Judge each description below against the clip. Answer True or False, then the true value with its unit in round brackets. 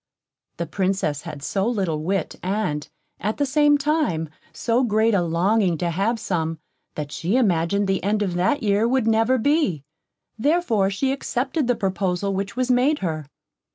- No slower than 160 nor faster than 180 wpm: True (165 wpm)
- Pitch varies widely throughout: True (5.9 semitones)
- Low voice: False (200 Hz)